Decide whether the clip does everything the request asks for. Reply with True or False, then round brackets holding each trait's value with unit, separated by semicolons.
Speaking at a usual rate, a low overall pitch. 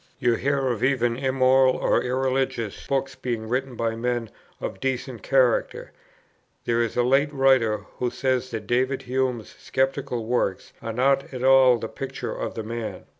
True (165 wpm; 125 Hz)